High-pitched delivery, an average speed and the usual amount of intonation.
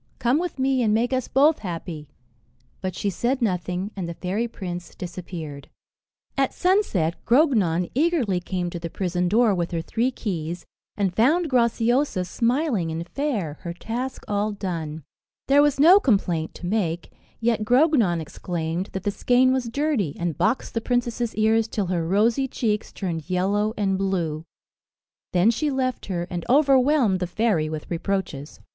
No: high, 205 Hz; average, 160 wpm; wide, 6.1 semitones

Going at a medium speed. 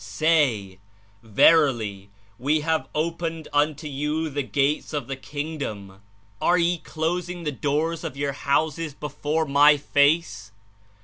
No: slow, 125 wpm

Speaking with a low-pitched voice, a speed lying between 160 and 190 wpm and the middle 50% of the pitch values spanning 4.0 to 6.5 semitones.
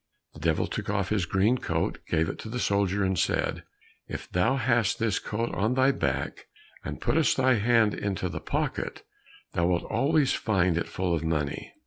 Yes: low, 100 Hz; average, 185 wpm; average, 5.2 semitones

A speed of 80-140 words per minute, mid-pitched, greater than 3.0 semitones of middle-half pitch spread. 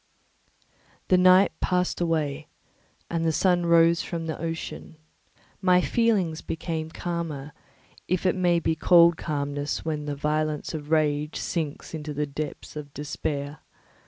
No: slow, 135 wpm; medium, 160 Hz; narrow, 2.4 semitones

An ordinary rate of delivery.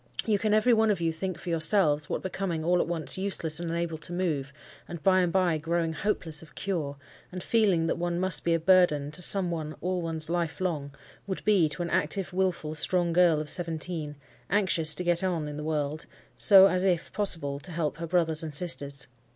No: fast, 215 wpm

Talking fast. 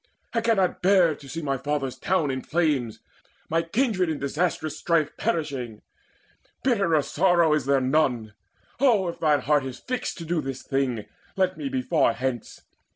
No: average, 165 wpm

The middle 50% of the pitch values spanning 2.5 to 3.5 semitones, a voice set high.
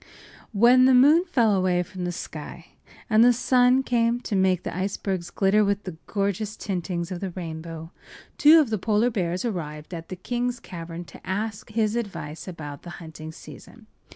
No: average, 5.1 semitones; high, 195 Hz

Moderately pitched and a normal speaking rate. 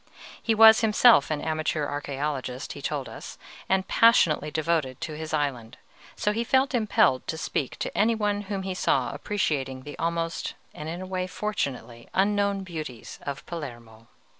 Yes: medium, 160 Hz; average, 165 wpm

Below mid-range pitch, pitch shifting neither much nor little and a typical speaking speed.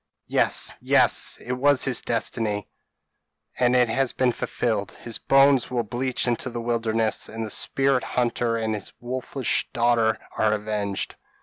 No: low, 120 Hz; narrow, 2.3 semitones; average, 145 wpm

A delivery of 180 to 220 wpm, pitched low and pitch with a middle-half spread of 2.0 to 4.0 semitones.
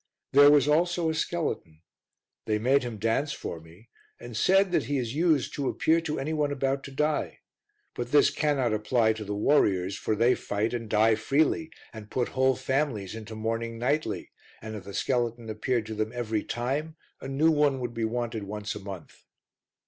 No: average, 190 wpm; low, 120 Hz; average, 4.9 semitones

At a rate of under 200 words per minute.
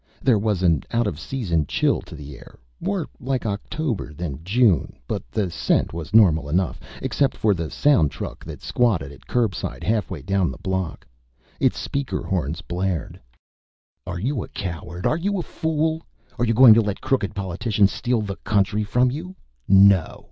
Yes: average, 175 wpm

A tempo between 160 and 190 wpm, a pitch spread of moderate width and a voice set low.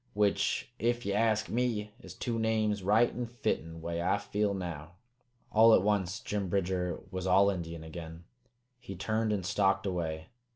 Yes: average, 165 wpm; average, 3.6 semitones; low, 100 Hz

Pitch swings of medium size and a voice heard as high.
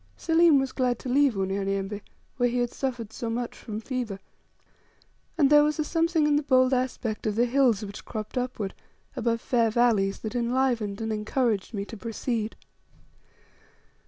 Yes: average, 3.5 semitones; high, 240 Hz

